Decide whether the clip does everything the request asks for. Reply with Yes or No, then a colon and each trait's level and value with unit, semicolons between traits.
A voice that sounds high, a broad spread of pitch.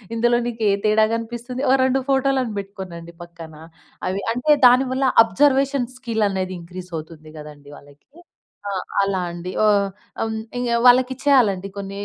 Yes: high, 220 Hz; wide, 5.7 semitones